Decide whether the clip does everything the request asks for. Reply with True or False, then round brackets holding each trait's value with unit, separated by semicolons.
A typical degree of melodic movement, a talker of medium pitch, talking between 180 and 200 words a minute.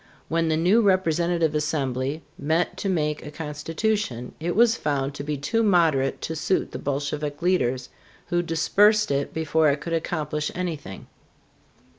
False (3.2 semitones; 160 Hz; 150 wpm)